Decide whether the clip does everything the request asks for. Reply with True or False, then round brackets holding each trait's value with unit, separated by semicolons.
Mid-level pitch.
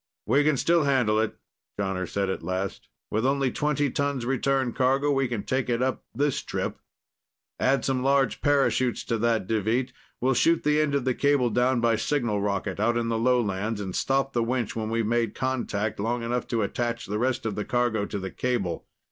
False (120 Hz)